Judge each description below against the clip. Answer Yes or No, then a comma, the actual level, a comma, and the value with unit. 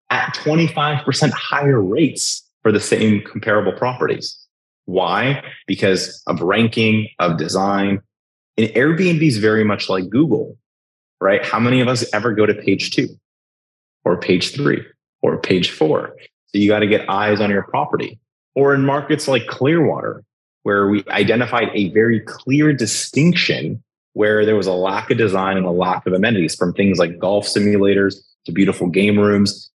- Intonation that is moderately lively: Yes, average, 4.3 semitones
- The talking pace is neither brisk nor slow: Yes, average, 160 wpm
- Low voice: Yes, low, 105 Hz